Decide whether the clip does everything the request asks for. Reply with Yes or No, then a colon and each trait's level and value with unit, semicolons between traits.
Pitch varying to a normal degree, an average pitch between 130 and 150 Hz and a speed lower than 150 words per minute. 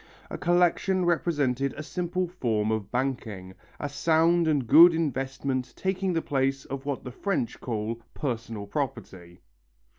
No: wide, 6.1 semitones; low, 135 Hz; average, 140 wpm